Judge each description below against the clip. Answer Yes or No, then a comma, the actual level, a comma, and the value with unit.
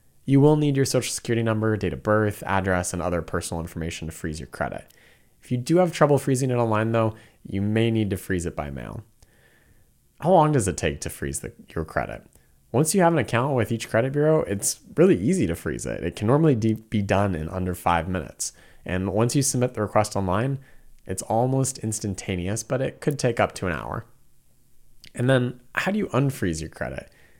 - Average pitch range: No, wide, 5.8 semitones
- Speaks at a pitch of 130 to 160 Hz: No, low, 110 Hz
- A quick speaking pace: Yes, fast, 210 wpm